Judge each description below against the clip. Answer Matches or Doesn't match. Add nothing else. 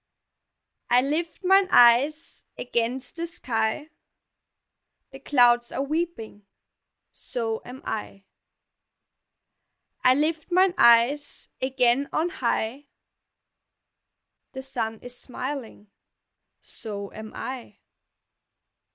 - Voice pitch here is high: Matches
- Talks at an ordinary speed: Doesn't match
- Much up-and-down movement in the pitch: Doesn't match